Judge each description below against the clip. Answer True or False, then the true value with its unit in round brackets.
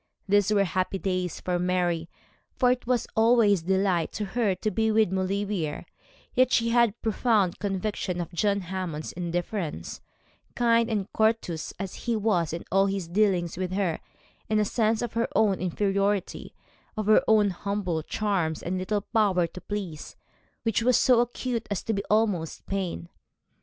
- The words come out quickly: False (165 wpm)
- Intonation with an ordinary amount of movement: True (3.4 semitones)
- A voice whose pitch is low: False (200 Hz)